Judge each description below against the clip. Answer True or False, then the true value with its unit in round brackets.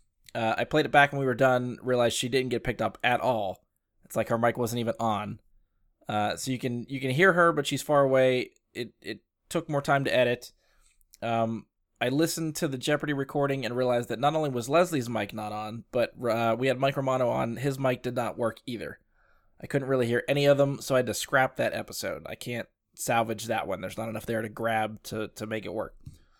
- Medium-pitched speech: False (125 Hz)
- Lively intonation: False (3.7 semitones)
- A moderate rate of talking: False (235 wpm)